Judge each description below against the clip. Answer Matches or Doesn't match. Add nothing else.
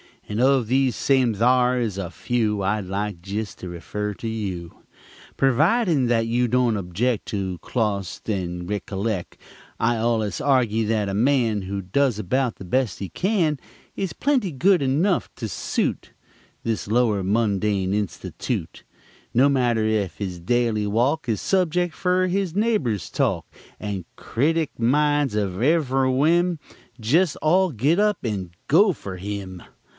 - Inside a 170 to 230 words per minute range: Doesn't match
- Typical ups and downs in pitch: Doesn't match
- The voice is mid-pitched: Doesn't match